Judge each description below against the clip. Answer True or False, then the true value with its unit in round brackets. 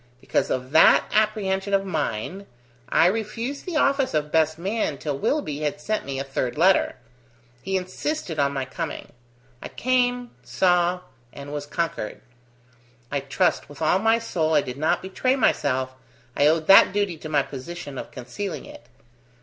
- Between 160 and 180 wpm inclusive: True (165 wpm)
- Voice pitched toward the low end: False (170 Hz)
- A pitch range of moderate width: False (6.5 semitones)